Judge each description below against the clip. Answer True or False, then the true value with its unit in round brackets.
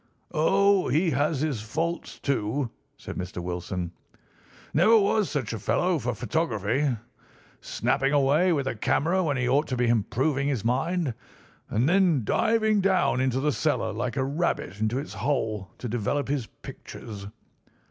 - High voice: False (135 Hz)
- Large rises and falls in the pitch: True (5.9 semitones)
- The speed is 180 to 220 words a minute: False (155 wpm)